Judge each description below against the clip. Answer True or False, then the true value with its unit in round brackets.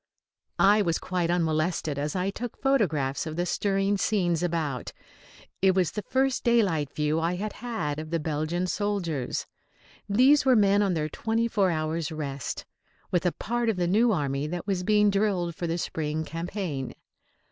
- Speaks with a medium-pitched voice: True (175 Hz)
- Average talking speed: True (170 wpm)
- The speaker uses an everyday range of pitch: True (4.7 semitones)